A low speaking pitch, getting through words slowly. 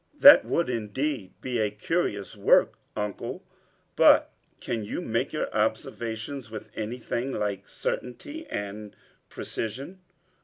Yes: low, 115 Hz; slow, 115 wpm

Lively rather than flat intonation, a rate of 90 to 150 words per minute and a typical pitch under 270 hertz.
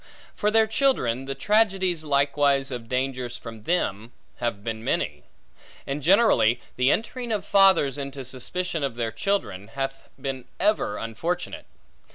Yes: wide, 7.5 semitones; average, 140 wpm; medium, 140 Hz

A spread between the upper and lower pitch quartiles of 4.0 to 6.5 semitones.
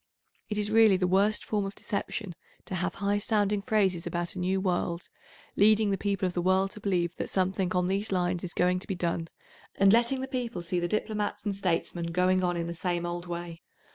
No: average, 2.7 semitones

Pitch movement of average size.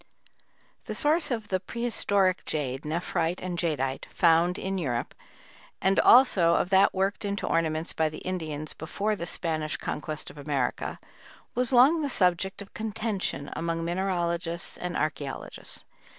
Yes: average, 4.0 semitones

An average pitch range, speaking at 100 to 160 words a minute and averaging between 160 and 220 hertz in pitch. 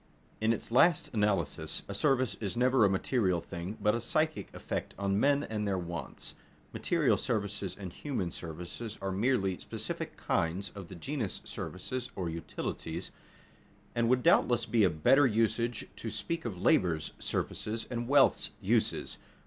No: average, 4.8 semitones; average, 155 wpm; low, 105 Hz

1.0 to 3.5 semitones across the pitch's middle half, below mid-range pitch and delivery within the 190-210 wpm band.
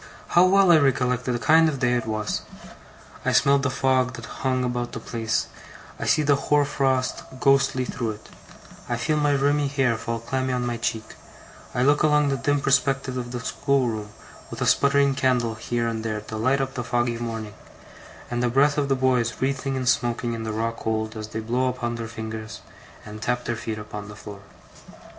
Yes: average, 3.1 semitones; low, 125 Hz; average, 200 wpm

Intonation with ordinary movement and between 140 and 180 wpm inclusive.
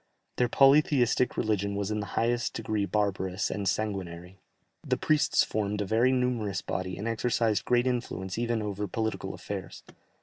Yes: average, 3.2 semitones; average, 155 wpm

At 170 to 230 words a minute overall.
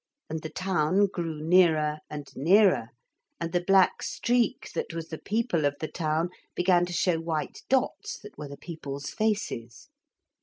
No: average, 160 wpm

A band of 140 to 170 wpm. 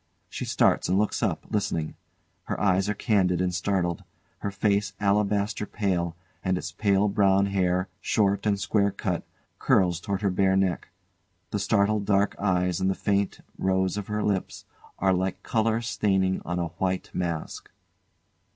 Yes: average, 160 wpm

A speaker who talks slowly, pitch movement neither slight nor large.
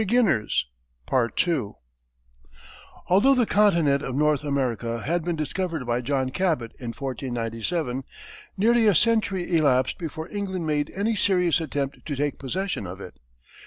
No: slow, 125 wpm; wide, 6.1 semitones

